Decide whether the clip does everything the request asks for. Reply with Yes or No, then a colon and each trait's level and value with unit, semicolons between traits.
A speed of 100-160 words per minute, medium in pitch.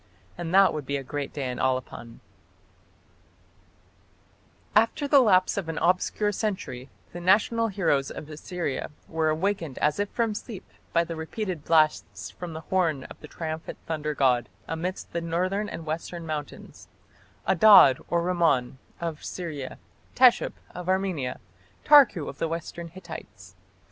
Yes: average, 145 wpm; medium, 165 Hz